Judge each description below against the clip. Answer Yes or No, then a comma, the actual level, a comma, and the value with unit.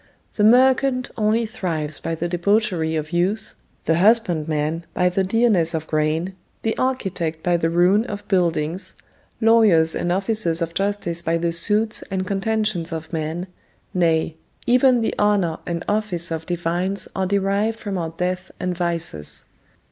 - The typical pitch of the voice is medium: Yes, medium, 180 Hz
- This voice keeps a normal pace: Yes, average, 155 wpm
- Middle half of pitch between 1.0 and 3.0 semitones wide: No, average, 4.1 semitones